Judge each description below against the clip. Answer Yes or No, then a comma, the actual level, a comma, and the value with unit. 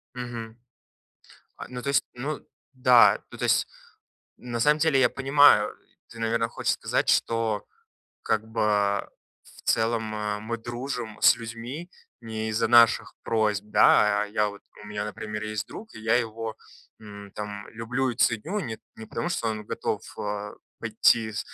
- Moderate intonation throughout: No, narrow, 2.2 semitones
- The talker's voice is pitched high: No, low, 115 Hz